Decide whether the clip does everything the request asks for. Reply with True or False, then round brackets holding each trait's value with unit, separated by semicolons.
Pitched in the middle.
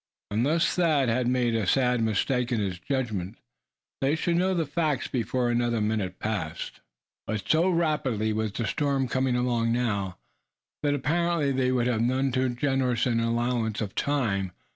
False (125 Hz)